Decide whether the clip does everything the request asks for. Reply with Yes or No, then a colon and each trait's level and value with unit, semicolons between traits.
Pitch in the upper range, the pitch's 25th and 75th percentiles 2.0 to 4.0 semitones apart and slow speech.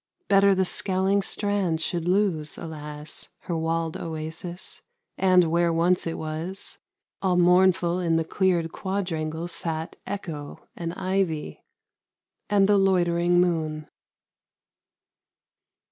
No: medium, 175 Hz; narrow, 2.6 semitones; slow, 110 wpm